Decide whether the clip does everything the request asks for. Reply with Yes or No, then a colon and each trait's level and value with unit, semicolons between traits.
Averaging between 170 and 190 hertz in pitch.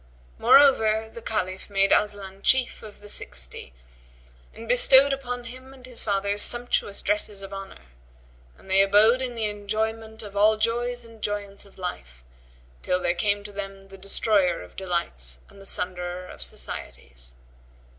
No: high, 205 Hz